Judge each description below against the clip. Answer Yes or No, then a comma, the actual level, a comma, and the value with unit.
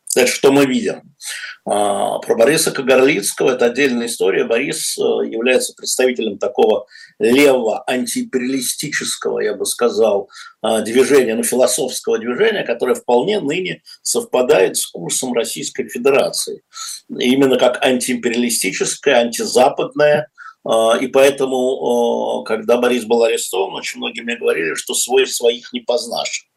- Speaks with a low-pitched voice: No, medium, 145 Hz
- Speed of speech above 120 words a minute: No, slow, 110 wpm